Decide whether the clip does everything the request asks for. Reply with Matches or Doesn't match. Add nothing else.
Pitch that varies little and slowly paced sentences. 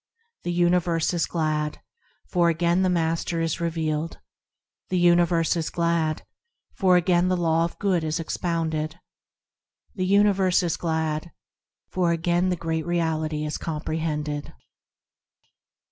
Matches